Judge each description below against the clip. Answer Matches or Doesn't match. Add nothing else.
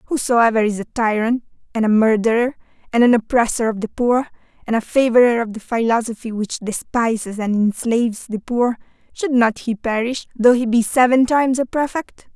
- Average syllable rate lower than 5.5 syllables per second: Matches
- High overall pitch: Matches